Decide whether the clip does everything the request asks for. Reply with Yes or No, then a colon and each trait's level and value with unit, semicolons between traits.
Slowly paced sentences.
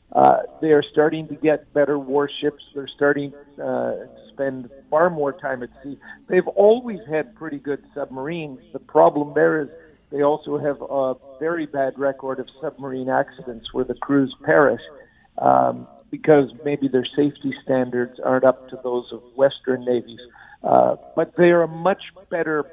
No: average, 160 wpm